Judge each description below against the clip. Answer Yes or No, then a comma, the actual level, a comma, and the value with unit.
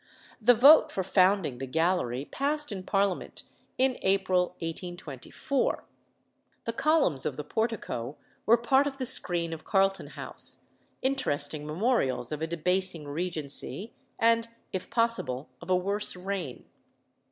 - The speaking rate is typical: No, slow, 130 wpm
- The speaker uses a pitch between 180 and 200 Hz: Yes, medium, 185 Hz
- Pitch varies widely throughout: Yes, wide, 6.8 semitones